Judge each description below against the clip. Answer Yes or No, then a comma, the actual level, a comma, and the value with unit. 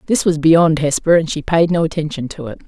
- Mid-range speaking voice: Yes, medium, 160 Hz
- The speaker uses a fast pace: Yes, fast, 245 wpm